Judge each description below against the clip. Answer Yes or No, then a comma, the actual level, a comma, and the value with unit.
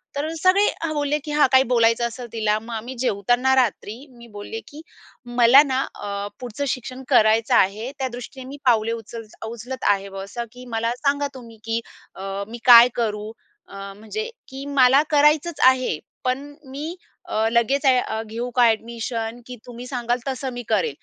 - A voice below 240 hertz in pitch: No, high, 245 Hz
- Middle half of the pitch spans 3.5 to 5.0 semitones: No, average, 3.0 semitones